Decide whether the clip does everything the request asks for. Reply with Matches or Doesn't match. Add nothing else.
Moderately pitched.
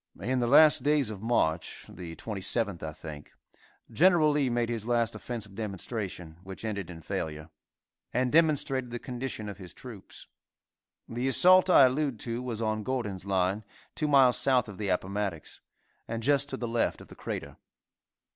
Doesn't match